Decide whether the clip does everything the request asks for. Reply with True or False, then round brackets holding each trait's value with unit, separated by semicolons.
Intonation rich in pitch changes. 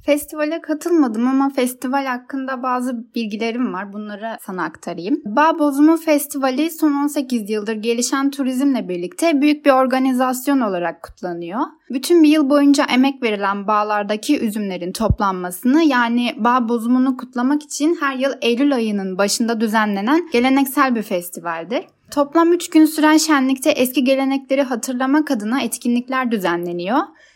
False (4.3 semitones)